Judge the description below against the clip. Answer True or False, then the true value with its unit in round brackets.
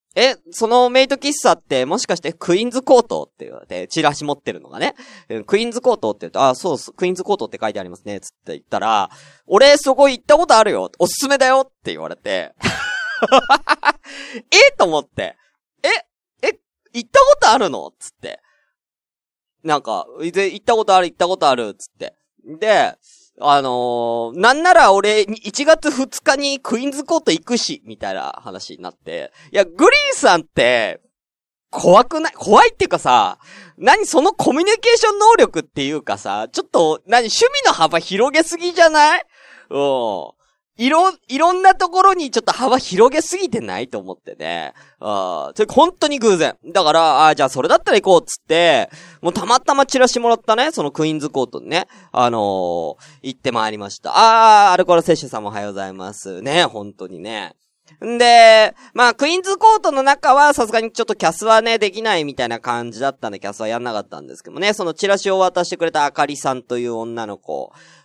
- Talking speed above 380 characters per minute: True (390 characters per minute)